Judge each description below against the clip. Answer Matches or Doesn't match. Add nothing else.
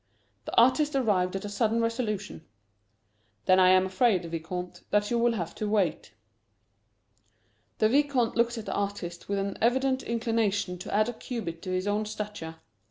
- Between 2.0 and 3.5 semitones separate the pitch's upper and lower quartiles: Doesn't match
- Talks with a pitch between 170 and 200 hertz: Doesn't match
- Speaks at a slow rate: Doesn't match